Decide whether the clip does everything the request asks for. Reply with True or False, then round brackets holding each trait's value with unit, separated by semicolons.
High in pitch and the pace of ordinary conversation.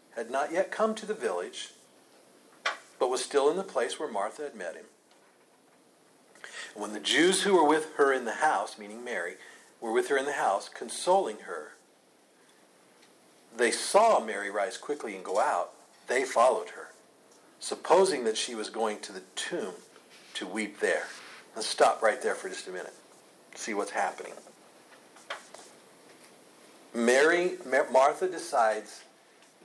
True (375 Hz; 150 wpm)